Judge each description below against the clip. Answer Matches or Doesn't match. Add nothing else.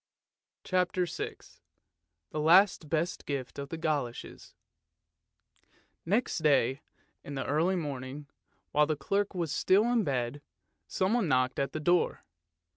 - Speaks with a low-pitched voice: Doesn't match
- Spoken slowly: Matches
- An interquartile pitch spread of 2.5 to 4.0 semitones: Doesn't match